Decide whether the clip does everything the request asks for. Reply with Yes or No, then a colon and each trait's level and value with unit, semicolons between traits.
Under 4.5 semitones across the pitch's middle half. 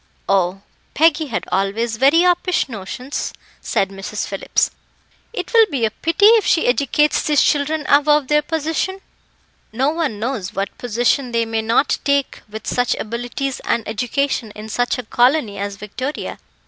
No: wide, 5.5 semitones